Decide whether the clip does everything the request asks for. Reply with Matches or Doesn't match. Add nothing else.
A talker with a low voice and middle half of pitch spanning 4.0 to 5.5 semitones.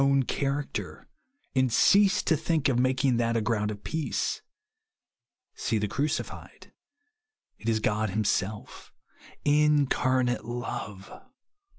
Matches